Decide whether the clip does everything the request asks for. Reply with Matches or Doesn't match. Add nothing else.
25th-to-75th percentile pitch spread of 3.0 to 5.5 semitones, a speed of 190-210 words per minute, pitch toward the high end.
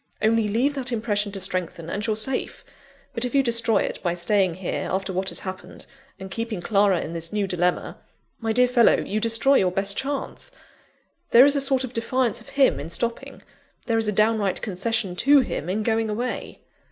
Matches